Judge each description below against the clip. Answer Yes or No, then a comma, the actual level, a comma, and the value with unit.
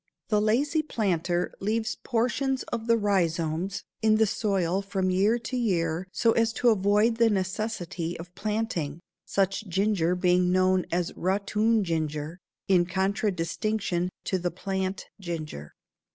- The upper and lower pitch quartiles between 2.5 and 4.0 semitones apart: Yes, average, 3.7 semitones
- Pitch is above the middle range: Yes, high, 195 Hz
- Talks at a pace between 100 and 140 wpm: Yes, slow, 135 wpm